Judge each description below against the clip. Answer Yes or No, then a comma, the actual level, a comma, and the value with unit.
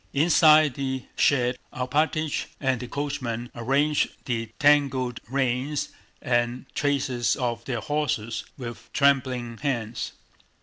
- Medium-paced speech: No, slow, 105 wpm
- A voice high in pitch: No, low, 130 Hz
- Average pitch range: Yes, average, 3.1 semitones